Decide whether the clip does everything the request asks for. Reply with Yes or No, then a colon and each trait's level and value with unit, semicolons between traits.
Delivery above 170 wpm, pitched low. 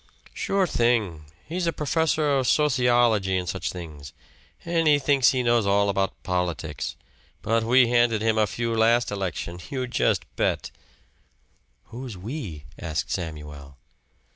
No: average, 140 wpm; low, 115 Hz